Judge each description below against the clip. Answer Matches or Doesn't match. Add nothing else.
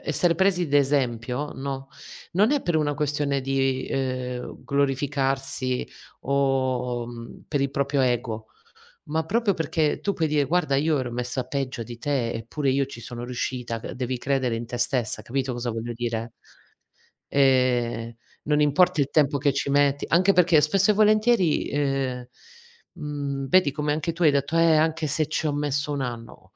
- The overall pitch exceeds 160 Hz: Doesn't match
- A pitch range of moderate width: Matches